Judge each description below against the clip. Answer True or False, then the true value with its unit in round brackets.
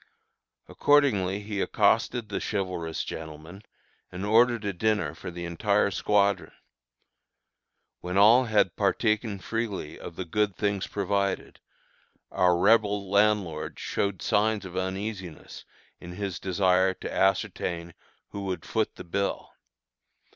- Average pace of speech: False (120 wpm)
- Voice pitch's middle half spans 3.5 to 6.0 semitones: False (2.6 semitones)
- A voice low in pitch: True (100 Hz)